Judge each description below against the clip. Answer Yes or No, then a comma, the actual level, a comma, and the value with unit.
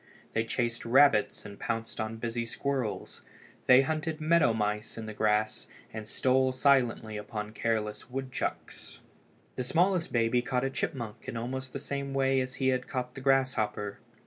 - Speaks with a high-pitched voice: No, low, 125 Hz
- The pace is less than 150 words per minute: No, average, 160 wpm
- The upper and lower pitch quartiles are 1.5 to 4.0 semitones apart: Yes, average, 3.3 semitones